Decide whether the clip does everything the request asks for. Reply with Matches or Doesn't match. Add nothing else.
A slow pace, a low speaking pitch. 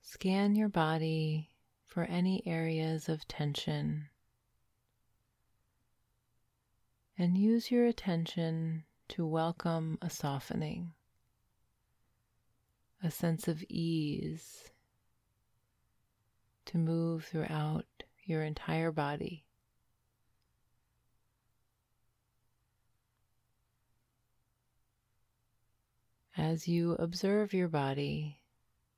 Matches